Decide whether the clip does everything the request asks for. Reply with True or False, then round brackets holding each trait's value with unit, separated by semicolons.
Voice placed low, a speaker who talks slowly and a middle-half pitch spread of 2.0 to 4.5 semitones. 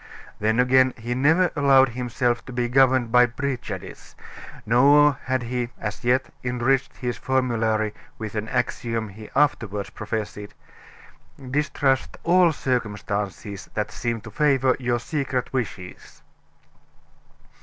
True (125 Hz; 120 wpm; 3.1 semitones)